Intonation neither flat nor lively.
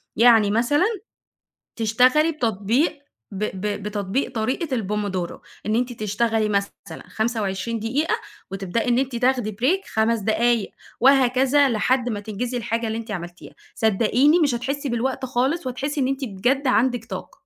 Yes: average, 3.6 semitones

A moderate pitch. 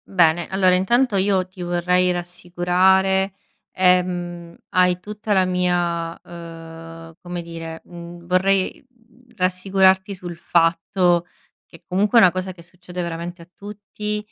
Yes: medium, 180 Hz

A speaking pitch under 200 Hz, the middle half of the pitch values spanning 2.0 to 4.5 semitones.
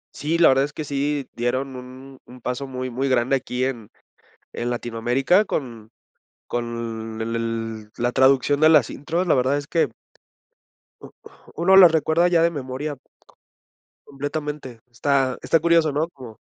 Yes: low, 135 Hz; average, 3.7 semitones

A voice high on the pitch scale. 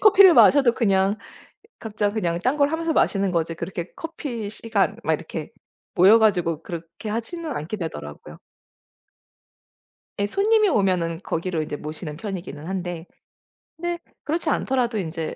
Yes: high, 200 Hz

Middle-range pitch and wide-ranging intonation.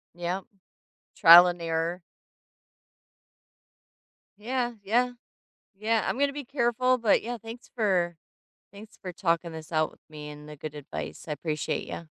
Yes: medium, 180 Hz; wide, 6.4 semitones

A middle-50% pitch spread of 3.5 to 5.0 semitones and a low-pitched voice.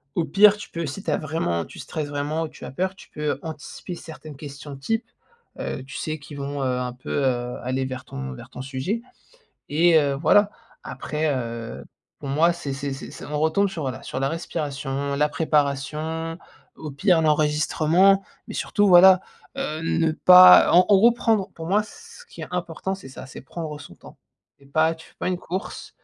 No: average, 4.1 semitones; medium, 155 Hz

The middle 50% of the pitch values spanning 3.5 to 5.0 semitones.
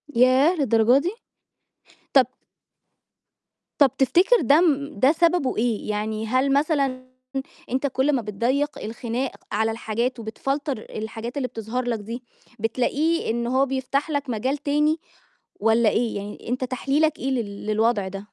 Yes: average, 4.0 semitones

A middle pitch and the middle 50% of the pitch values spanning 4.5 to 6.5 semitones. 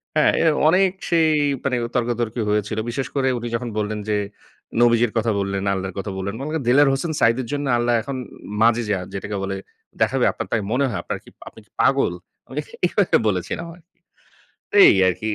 No: low, 120 Hz; average, 4.8 semitones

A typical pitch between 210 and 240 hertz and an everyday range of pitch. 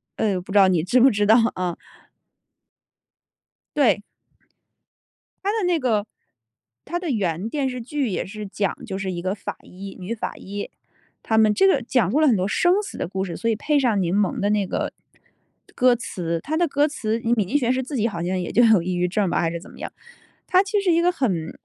No: high, 215 Hz; wide, 6.1 semitones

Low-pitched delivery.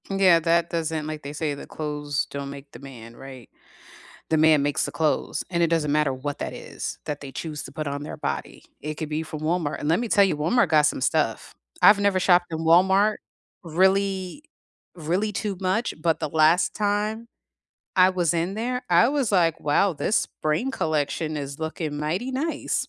No: medium, 160 Hz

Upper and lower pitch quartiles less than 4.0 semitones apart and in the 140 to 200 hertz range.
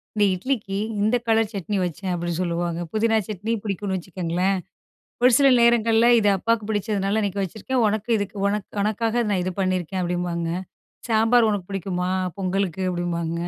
Yes: average, 3.4 semitones; high, 195 Hz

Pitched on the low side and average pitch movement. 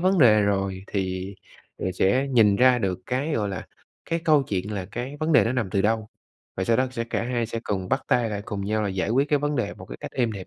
Yes: low, 110 Hz; average, 4.6 semitones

